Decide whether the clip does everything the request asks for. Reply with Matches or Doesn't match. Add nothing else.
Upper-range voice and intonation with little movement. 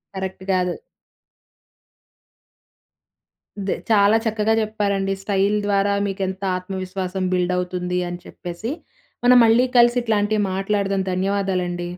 Matches